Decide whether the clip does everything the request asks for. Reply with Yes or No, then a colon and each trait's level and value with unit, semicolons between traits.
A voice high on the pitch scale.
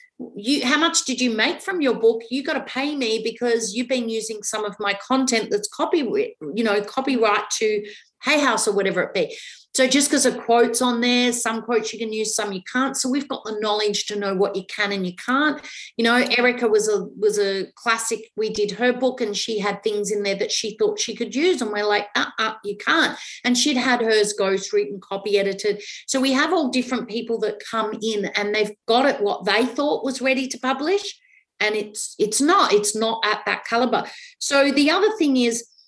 Yes: high, 230 Hz